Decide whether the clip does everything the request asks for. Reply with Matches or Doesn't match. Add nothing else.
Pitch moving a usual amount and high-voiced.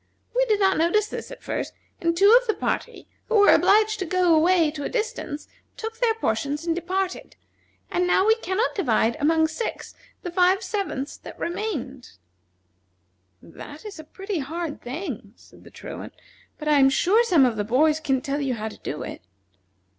Doesn't match